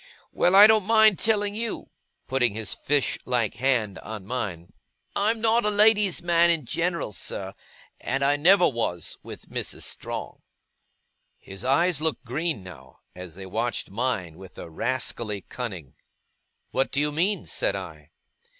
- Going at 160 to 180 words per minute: No, average, 150 wpm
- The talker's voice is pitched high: No, low, 135 Hz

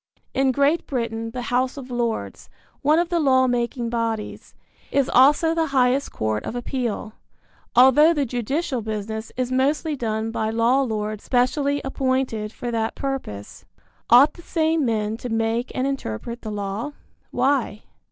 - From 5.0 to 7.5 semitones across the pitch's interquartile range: No, average, 3.5 semitones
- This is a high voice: Yes, high, 245 Hz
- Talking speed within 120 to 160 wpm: Yes, average, 150 wpm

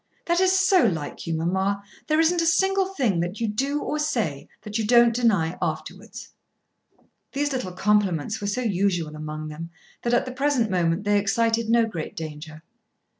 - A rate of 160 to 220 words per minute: Yes, average, 175 wpm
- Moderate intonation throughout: No, wide, 7.3 semitones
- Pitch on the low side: No, high, 210 Hz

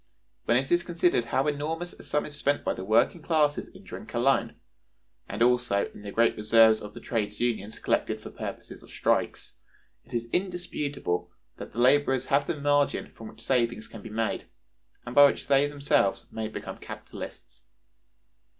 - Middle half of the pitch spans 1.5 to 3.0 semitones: No, average, 4.5 semitones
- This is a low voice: Yes, low, 125 Hz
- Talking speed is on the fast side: No, average, 175 wpm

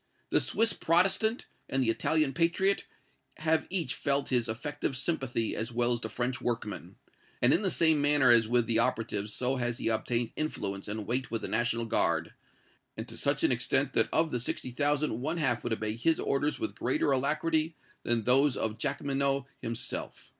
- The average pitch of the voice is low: Yes, low, 130 Hz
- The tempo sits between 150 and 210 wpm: Yes, average, 185 wpm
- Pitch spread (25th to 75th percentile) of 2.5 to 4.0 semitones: No, average, 4.4 semitones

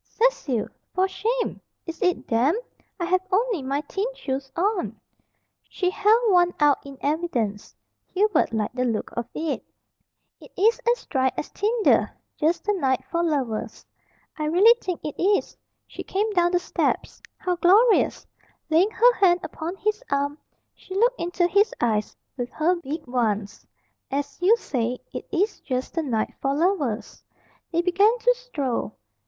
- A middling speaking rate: Yes, average, 160 wpm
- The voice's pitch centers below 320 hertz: No, very high, 345 Hz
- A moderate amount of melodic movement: No, wide, 6.9 semitones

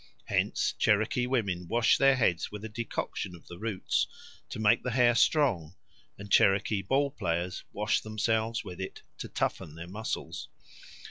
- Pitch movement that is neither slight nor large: Yes, average, 4.2 semitones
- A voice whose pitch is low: Yes, low, 105 Hz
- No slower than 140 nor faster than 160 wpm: Yes, average, 155 wpm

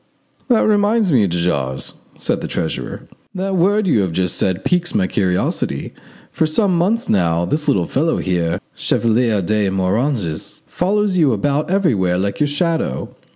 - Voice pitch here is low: Yes, low, 125 Hz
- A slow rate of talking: No, average, 155 wpm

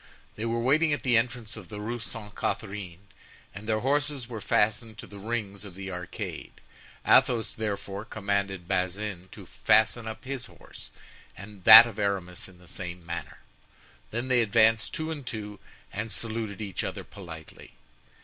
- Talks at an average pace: Yes, average, 165 wpm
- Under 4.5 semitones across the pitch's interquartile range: Yes, average, 3.0 semitones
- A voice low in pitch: Yes, low, 105 Hz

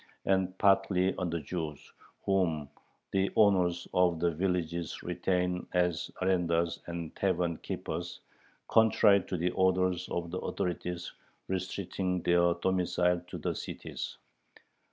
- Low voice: Yes, very low, 90 Hz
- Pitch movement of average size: No, narrow, 1.5 semitones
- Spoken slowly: Yes, slow, 120 wpm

